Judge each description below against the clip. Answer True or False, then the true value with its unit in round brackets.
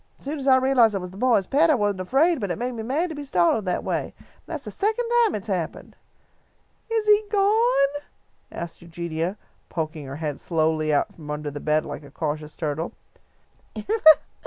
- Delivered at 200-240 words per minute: True (205 wpm)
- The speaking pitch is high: True (195 Hz)